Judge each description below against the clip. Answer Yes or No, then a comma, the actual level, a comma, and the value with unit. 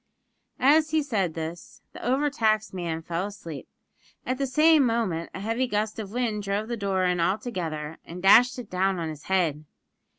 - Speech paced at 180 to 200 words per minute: Yes, average, 185 wpm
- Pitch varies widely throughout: Yes, wide, 6.0 semitones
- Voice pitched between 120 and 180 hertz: No, high, 200 Hz